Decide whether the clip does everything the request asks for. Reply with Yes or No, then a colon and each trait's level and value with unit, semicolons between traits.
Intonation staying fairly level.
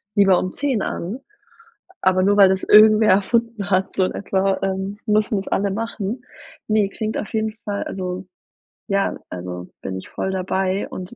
Yes: narrow, 2.3 semitones